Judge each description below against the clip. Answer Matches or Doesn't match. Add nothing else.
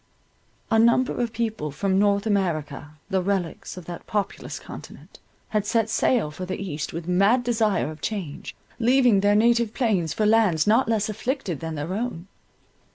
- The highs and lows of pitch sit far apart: Doesn't match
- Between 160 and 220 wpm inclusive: Matches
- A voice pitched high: Matches